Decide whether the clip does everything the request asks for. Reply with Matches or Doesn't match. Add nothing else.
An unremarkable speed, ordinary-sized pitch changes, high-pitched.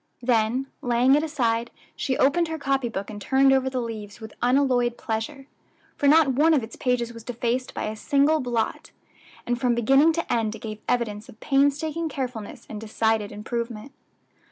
Matches